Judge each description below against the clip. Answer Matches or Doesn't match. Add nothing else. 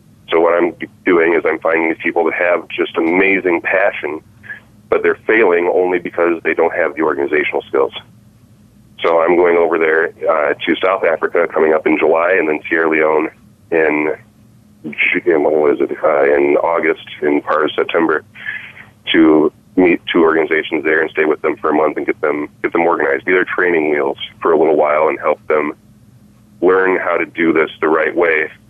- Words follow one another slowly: Doesn't match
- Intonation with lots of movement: Matches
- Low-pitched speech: Matches